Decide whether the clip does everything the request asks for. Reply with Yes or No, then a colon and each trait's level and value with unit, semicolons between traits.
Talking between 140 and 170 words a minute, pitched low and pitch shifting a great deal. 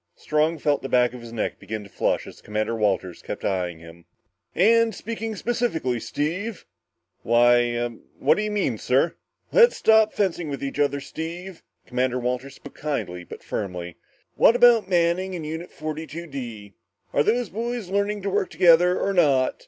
No: average, 165 wpm; medium, 155 Hz; wide, 8.1 semitones